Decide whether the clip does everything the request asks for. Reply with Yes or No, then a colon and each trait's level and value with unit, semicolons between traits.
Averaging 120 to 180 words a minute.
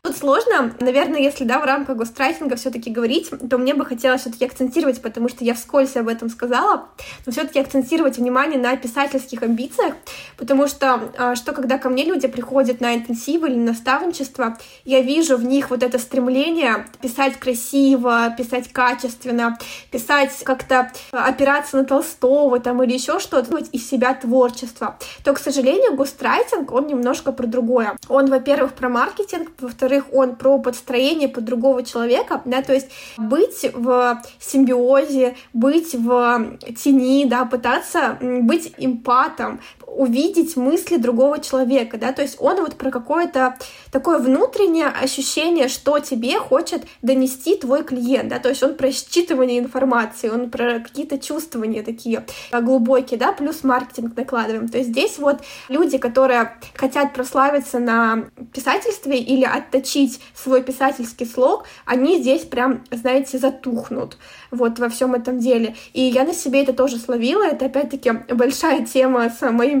Yes: average, 150 wpm